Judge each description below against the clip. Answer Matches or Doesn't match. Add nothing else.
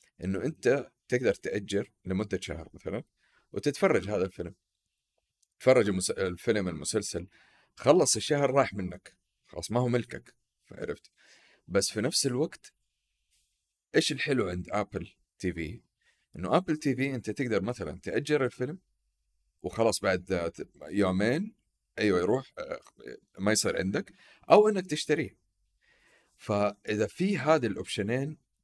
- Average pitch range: Doesn't match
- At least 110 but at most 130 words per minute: Matches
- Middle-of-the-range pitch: Doesn't match